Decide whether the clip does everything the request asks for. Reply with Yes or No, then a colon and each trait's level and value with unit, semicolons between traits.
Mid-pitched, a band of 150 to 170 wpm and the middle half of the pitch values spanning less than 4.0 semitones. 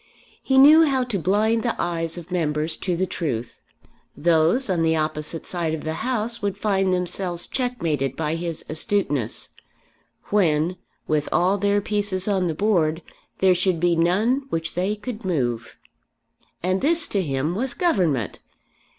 No: medium, 180 Hz; average, 155 wpm; average, 4.5 semitones